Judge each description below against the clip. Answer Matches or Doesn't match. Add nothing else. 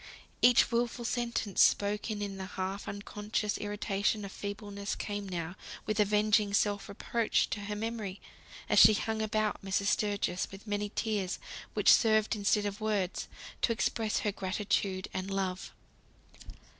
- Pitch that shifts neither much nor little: Doesn't match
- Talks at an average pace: Matches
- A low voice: Doesn't match